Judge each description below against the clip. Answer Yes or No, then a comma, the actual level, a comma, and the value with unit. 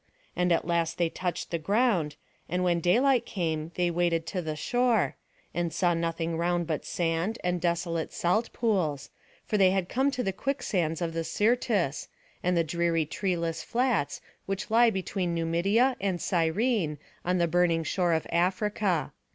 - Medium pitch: Yes, medium, 175 Hz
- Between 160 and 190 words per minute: Yes, average, 165 wpm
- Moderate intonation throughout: Yes, average, 3.4 semitones